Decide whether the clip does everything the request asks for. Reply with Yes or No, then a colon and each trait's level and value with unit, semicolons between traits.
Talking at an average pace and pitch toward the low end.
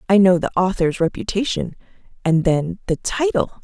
No: average, 150 wpm; high, 190 Hz